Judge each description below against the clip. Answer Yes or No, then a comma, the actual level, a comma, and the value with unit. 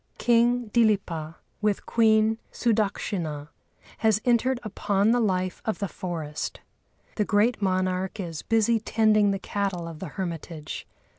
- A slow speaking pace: Yes, slow, 130 wpm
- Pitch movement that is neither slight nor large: Yes, average, 3.5 semitones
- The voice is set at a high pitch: Yes, high, 205 Hz